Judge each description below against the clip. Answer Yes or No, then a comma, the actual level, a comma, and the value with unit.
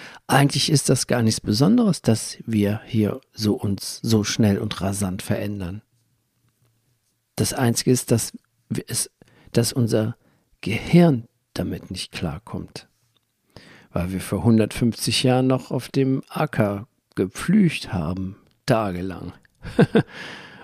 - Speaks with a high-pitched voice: No, low, 115 Hz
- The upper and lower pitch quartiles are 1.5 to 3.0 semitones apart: No, average, 3.9 semitones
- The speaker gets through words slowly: Yes, slow, 115 wpm